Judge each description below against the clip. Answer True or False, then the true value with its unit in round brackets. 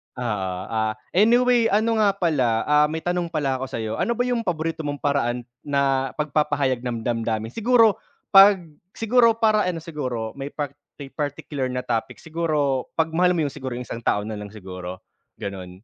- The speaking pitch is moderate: True (145 Hz)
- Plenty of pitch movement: True (7.0 semitones)